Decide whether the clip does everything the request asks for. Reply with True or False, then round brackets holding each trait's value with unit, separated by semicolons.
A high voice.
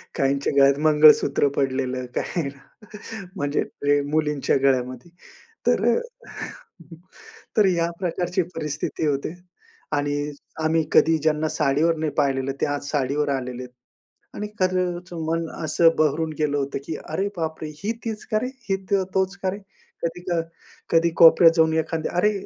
False (155 Hz)